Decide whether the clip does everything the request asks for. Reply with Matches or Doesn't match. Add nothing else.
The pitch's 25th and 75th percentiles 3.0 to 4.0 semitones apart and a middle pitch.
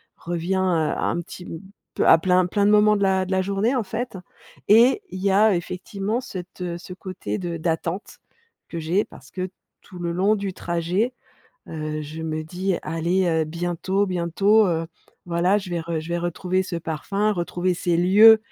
Doesn't match